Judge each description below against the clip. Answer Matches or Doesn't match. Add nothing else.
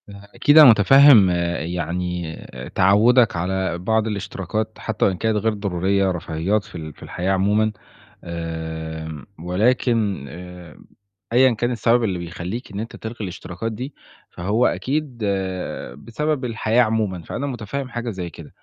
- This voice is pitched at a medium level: Doesn't match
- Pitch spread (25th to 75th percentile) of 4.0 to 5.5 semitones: Matches